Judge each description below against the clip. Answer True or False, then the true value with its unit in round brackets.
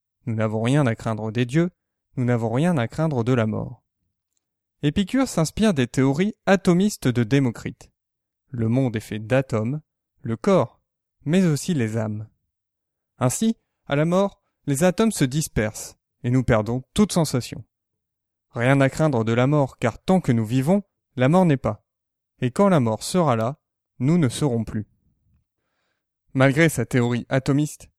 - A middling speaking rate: True (160 wpm)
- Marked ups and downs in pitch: True (5.7 semitones)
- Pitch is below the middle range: True (125 Hz)